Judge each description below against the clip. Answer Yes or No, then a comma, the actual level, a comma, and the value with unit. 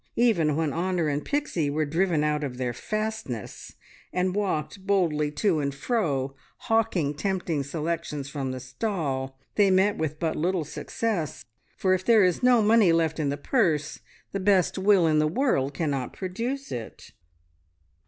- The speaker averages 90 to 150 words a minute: No, average, 160 wpm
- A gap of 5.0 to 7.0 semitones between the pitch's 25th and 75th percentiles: Yes, average, 5.3 semitones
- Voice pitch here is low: No, medium, 165 Hz